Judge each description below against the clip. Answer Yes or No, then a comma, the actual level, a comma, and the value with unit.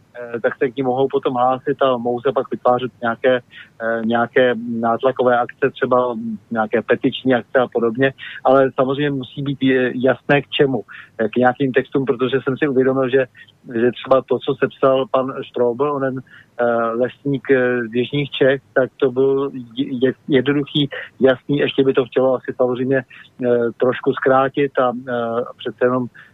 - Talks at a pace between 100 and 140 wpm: No, average, 150 wpm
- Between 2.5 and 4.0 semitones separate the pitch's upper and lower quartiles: No, narrow, 1.8 semitones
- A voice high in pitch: No, low, 130 Hz